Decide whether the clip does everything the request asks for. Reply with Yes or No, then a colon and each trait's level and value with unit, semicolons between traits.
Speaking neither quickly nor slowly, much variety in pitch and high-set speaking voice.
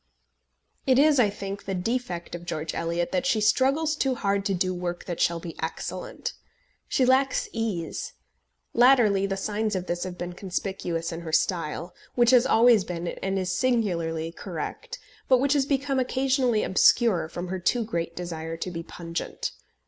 Yes: average, 170 wpm; wide, 6.1 semitones; high, 195 Hz